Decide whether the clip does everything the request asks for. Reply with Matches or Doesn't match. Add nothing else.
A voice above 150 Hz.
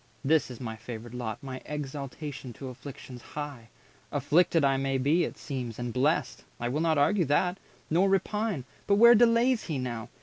Doesn't match